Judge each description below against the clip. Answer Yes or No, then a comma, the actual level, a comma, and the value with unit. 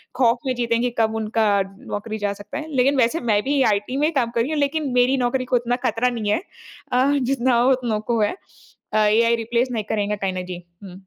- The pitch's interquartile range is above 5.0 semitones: No, average, 3.3 semitones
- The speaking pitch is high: Yes, high, 235 Hz